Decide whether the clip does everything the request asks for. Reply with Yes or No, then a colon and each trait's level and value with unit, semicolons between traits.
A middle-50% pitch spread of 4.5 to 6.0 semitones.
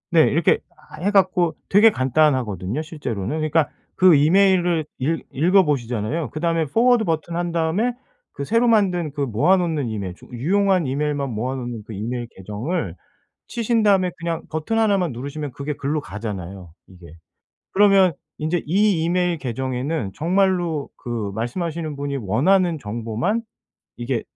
No: wide, 6.6 semitones